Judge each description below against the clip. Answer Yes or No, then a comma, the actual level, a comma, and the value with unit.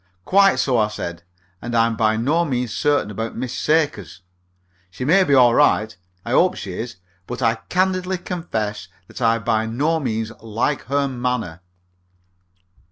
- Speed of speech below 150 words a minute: No, average, 160 wpm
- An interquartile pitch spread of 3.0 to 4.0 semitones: No, average, 5.0 semitones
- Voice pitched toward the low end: Yes, low, 120 Hz